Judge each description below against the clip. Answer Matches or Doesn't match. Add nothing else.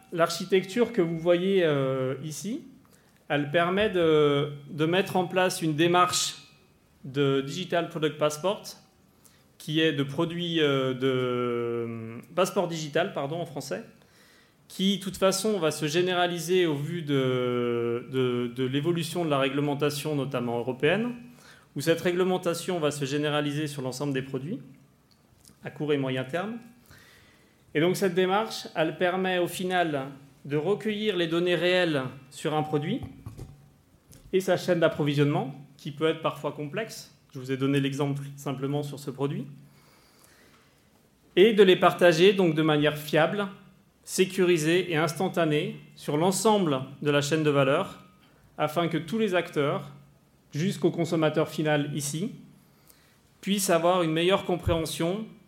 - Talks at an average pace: Doesn't match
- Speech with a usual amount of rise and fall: Matches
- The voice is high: Doesn't match